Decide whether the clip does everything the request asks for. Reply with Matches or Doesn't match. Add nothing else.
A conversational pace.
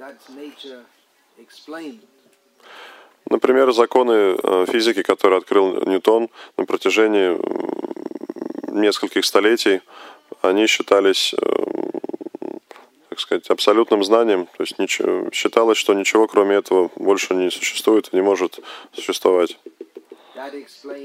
Doesn't match